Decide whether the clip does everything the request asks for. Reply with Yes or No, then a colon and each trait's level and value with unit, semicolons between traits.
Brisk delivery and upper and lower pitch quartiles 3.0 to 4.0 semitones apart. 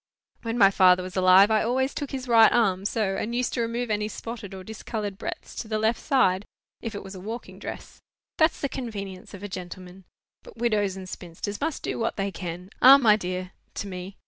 Yes: fast, 215 wpm; average, 3.7 semitones